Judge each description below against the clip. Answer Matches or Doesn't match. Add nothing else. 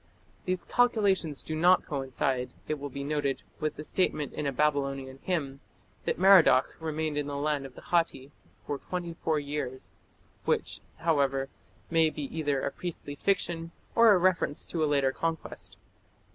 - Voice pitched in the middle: Matches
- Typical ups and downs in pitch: Matches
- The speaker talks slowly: Doesn't match